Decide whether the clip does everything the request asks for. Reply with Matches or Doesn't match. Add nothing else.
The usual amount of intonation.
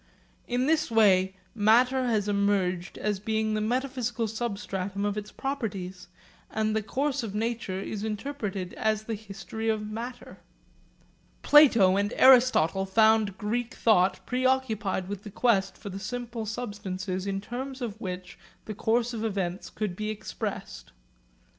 Matches